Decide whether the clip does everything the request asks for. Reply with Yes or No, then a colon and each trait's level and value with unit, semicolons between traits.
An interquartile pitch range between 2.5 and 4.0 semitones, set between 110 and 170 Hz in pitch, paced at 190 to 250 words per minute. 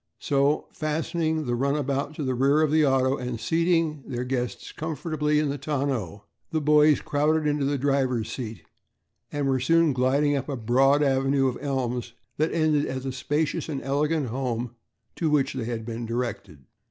No: average, 3.1 semitones; medium, 140 Hz; average, 175 wpm